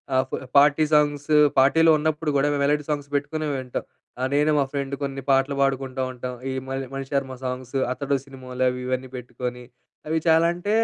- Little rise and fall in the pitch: Yes, narrow, 2.2 semitones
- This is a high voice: No, low, 135 Hz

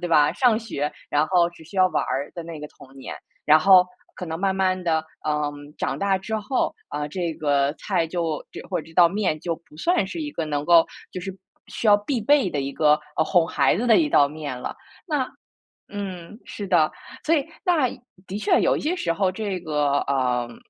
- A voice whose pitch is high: No, medium, 175 Hz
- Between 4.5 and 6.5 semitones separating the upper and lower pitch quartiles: Yes, average, 5.0 semitones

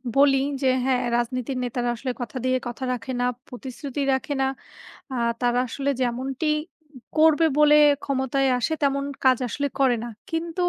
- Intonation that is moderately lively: No, narrow, 2.3 semitones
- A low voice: No, very high, 265 Hz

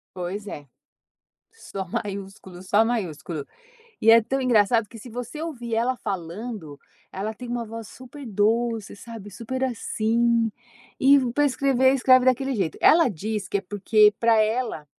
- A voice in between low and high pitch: No, high, 225 Hz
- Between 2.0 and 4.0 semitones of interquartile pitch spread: Yes, average, 3.7 semitones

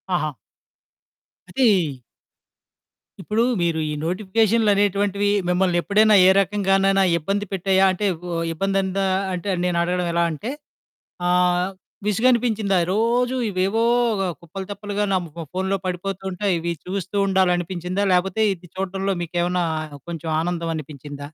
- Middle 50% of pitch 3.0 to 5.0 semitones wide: No, narrow, 2.4 semitones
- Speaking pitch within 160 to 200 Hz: Yes, high, 190 Hz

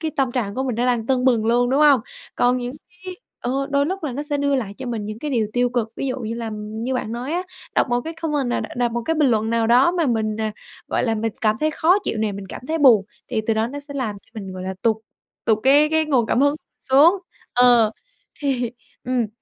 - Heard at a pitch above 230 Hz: Yes, high, 245 Hz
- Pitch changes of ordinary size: Yes, average, 4.0 semitones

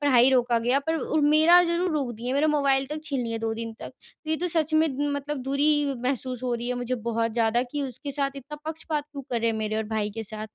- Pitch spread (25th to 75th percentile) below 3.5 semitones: No, average, 4.2 semitones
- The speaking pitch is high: Yes, very high, 270 Hz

